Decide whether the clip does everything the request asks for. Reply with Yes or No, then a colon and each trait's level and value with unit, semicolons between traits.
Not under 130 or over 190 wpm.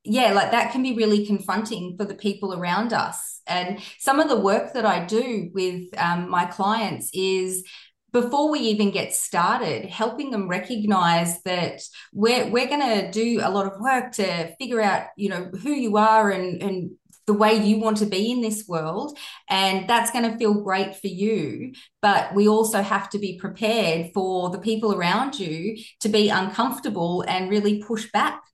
Yes: average, 185 wpm